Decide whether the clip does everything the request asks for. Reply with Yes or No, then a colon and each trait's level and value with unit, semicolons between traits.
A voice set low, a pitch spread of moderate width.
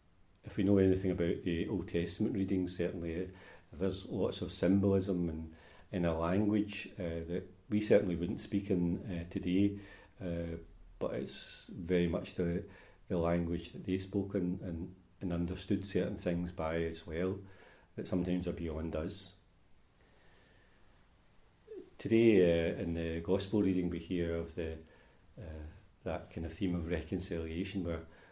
No: very low, 90 Hz; narrow, 2.3 semitones